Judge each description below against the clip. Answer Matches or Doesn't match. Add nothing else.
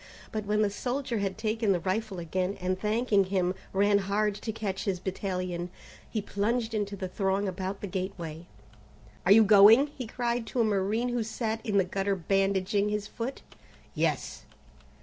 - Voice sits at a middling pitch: Doesn't match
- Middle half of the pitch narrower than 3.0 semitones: Matches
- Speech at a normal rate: Matches